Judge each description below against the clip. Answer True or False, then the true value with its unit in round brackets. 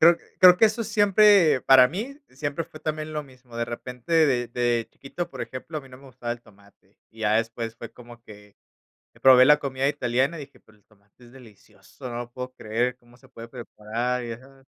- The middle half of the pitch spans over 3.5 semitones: True (4.0 semitones)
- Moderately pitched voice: False (125 Hz)